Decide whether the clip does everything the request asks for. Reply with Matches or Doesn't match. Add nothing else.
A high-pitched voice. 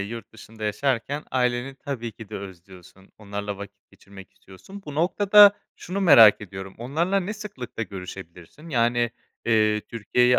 Doesn't match